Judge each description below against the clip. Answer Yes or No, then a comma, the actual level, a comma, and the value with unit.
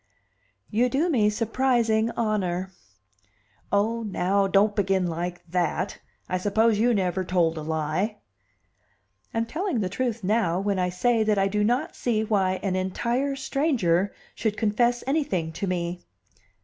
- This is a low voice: No, high, 205 Hz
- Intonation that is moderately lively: Yes, average, 4.1 semitones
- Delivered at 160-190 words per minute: No, average, 145 wpm